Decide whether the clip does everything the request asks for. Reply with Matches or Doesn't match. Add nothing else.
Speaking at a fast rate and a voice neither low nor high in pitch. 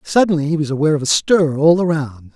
Matches